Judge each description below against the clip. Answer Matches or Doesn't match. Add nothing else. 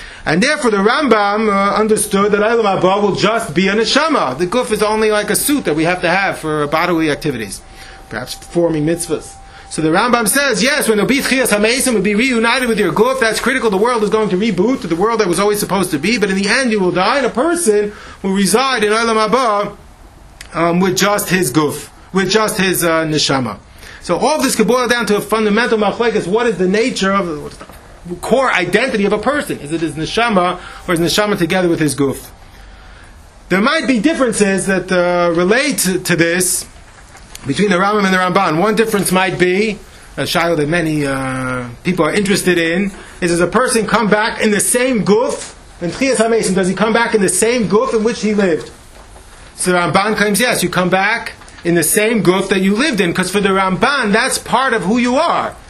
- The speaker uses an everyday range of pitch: Matches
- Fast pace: Matches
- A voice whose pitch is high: Matches